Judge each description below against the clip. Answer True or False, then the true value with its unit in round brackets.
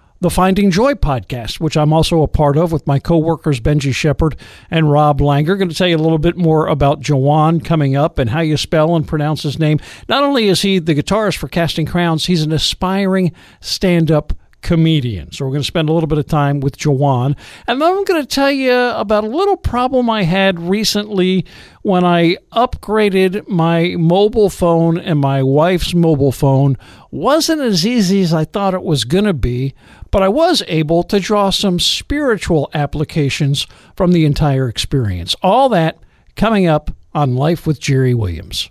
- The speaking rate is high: False (195 wpm)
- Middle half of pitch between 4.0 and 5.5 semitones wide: True (4.9 semitones)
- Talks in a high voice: False (165 Hz)